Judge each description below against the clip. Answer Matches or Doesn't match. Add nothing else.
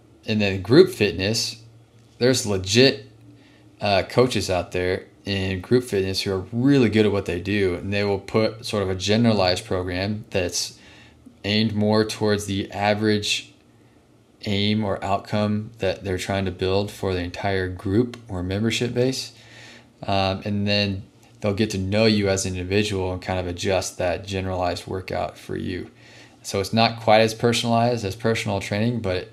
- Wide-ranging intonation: Doesn't match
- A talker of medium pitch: Doesn't match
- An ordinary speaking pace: Matches